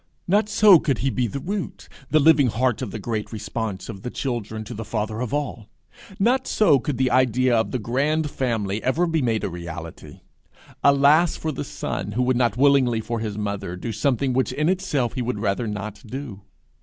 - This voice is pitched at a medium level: No, low, 125 Hz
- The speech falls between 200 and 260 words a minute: Yes, fast, 205 wpm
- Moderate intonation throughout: Yes, average, 4.6 semitones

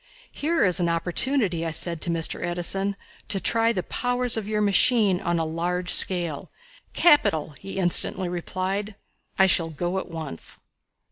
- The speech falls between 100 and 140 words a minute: No, average, 155 wpm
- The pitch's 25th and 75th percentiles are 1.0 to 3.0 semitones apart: No, average, 3.6 semitones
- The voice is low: No, medium, 180 Hz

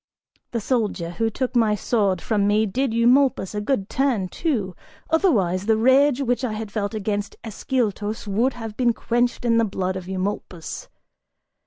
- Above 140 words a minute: Yes, average, 165 wpm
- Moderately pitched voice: No, high, 220 Hz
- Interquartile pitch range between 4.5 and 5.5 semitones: No, average, 3.5 semitones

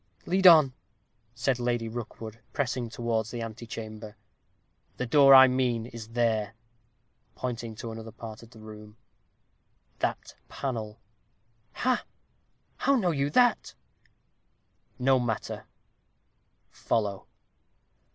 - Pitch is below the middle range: Yes, low, 115 Hz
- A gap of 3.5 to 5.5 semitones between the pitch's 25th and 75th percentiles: No, average, 2.8 semitones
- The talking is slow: Yes, slow, 110 wpm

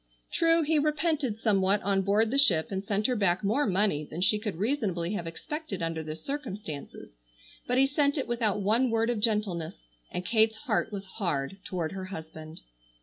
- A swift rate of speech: No, average, 185 wpm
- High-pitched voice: Yes, high, 210 Hz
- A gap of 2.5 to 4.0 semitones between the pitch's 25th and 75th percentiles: No, average, 5.2 semitones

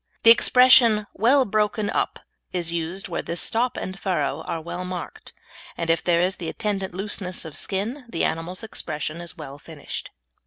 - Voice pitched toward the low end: No, medium, 185 Hz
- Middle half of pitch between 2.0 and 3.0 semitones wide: No, average, 4.2 semitones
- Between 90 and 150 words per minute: No, average, 170 wpm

